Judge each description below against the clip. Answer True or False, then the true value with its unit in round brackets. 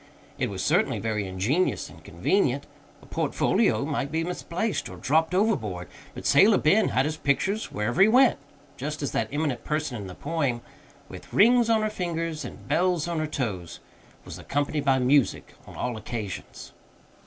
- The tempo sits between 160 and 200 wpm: True (170 wpm)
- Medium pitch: True (150 Hz)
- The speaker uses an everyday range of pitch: False (6.8 semitones)